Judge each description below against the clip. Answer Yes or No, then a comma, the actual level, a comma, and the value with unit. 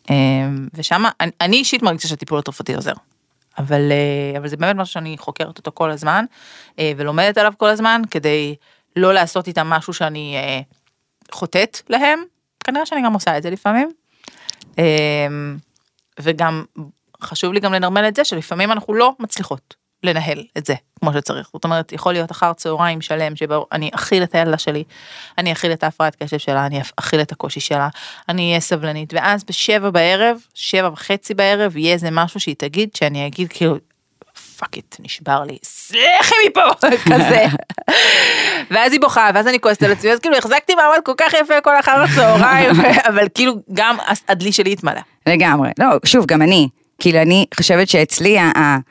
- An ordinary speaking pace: No, fast, 170 wpm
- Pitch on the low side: No, medium, 170 Hz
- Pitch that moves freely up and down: Yes, wide, 5.8 semitones